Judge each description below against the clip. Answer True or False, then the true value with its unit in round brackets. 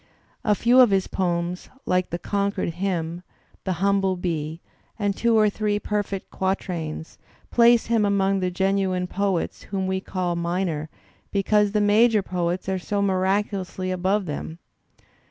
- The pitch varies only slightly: True (2.3 semitones)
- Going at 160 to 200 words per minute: False (145 wpm)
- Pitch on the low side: False (190 Hz)